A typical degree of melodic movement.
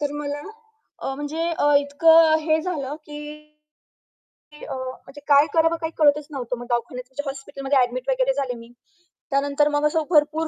No: narrow, 2.3 semitones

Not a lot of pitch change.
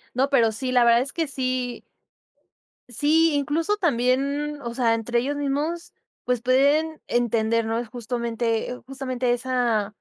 No: average, 3.3 semitones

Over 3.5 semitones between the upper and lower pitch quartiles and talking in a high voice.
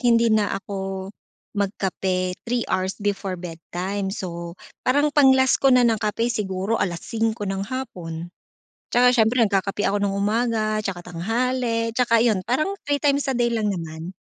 Yes: average, 4.1 semitones; high, 210 Hz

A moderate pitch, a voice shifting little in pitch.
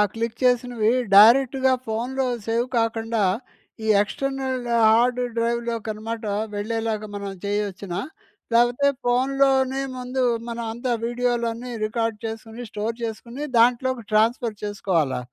No: high, 230 Hz; narrow, 2.1 semitones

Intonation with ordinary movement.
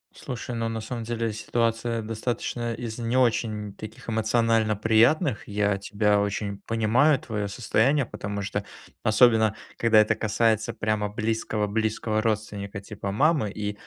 No: narrow, 1.8 semitones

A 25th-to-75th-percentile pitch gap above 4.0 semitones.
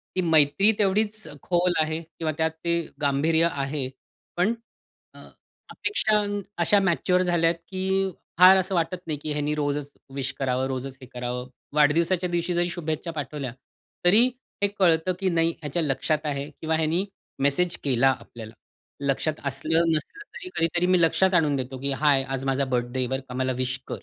Yes: average, 4.4 semitones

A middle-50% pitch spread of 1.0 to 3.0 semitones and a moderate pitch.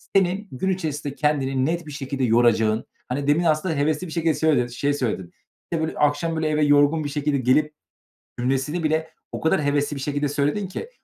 Yes: narrow, 2.5 semitones; medium, 145 Hz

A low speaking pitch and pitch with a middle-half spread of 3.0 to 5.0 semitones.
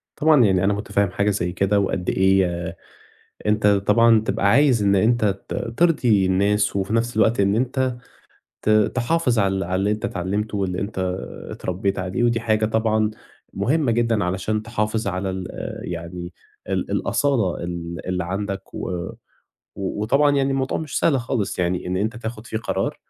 Yes: low, 105 Hz; average, 3.5 semitones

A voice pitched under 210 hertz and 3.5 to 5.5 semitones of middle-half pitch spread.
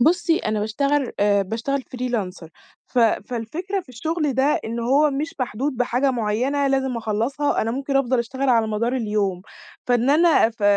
No: very high, 250 Hz; average, 3.9 semitones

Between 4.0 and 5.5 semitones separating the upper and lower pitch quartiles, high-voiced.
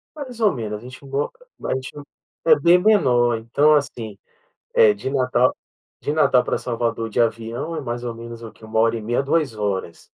No: average, 4.3 semitones; low, 120 Hz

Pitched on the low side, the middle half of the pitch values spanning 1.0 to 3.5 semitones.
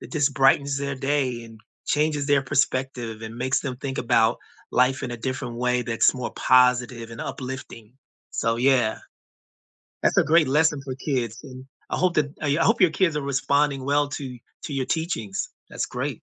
Yes: low, 130 Hz; average, 2.7 semitones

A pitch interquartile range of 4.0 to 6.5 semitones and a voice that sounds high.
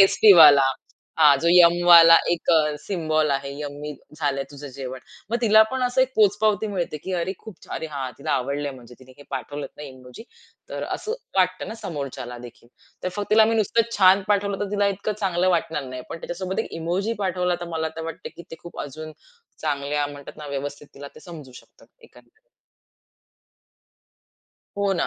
No: wide, 5.5 semitones; medium, 165 Hz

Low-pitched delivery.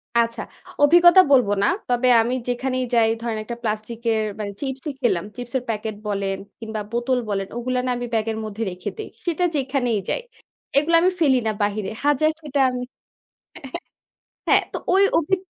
No: high, 245 Hz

